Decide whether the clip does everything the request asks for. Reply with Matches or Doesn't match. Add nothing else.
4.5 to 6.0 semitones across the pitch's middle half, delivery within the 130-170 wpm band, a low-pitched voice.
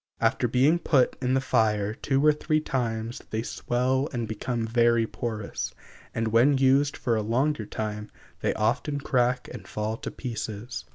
Doesn't match